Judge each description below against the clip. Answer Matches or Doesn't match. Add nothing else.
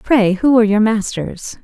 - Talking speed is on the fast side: Doesn't match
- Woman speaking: Matches